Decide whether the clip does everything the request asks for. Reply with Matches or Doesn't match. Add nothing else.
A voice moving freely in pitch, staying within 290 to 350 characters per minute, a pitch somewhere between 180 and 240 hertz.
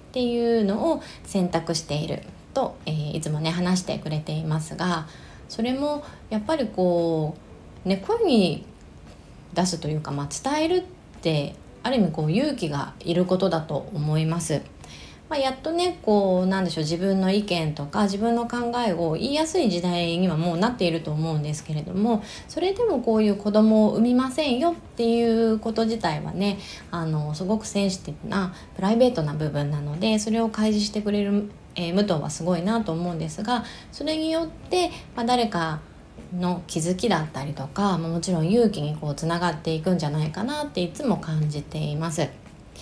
Doesn't match